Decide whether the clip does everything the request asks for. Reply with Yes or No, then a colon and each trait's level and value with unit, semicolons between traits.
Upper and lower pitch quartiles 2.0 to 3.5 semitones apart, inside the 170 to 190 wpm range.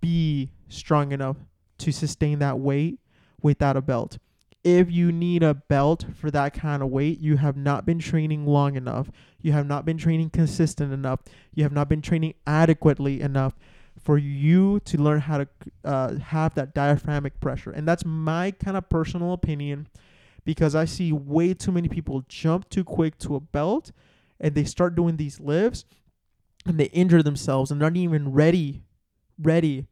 Yes: narrow, 2.5 semitones; average, 175 wpm